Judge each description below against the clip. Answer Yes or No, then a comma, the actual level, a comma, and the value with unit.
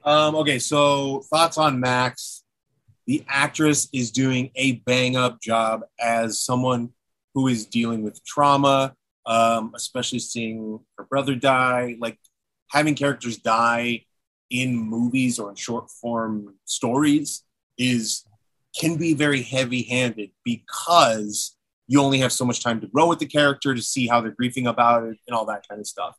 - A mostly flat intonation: No, average, 3.2 semitones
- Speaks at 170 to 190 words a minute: No, average, 160 wpm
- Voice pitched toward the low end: Yes, low, 125 Hz